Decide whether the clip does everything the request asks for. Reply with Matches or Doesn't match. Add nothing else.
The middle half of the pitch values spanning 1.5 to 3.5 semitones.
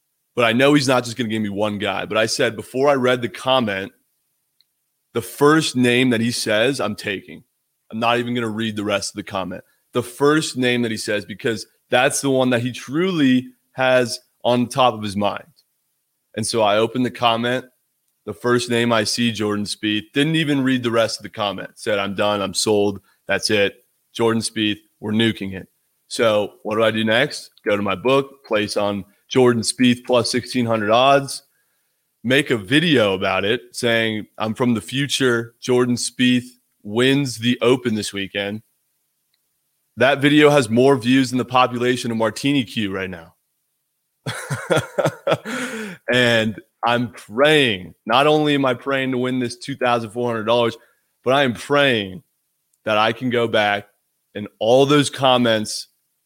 Matches